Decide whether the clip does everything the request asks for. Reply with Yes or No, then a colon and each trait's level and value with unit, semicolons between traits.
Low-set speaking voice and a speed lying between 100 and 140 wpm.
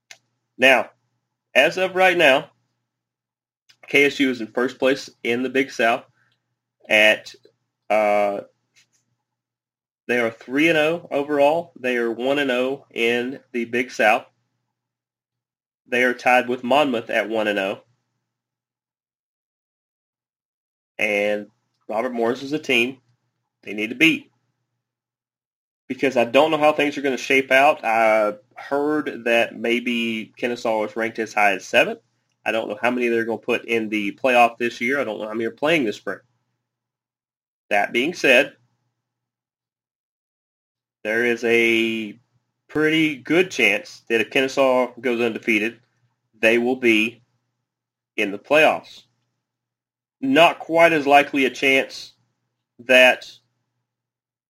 Yes: low, 120 Hz; slow, 135 wpm